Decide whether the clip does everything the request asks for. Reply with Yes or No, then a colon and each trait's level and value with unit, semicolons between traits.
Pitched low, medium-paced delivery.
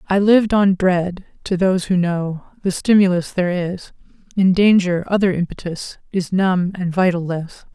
No: medium, 185 Hz; average, 165 wpm